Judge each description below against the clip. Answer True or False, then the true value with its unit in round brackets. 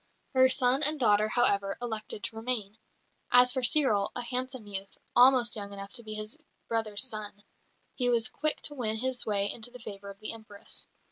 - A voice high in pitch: True (225 Hz)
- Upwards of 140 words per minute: True (190 wpm)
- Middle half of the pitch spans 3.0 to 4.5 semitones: True (3.4 semitones)